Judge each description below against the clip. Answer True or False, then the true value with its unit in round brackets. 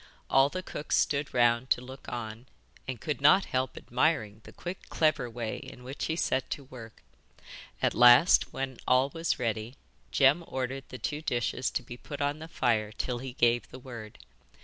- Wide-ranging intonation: False (3.1 semitones)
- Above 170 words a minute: True (185 wpm)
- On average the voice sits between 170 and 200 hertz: False (130 Hz)